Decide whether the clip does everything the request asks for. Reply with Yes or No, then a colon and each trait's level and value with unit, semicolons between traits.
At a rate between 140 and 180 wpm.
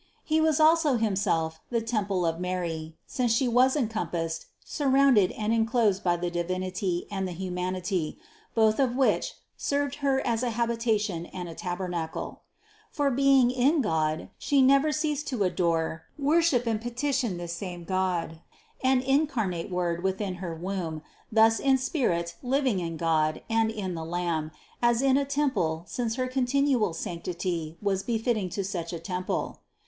Yes: average, 165 wpm